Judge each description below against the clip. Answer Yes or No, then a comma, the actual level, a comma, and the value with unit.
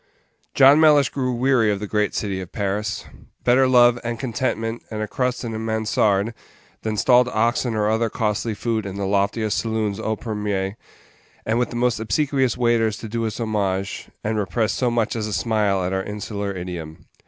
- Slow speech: No, average, 190 wpm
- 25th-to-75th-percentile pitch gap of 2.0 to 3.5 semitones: Yes, narrow, 2.6 semitones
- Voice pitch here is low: Yes, low, 110 Hz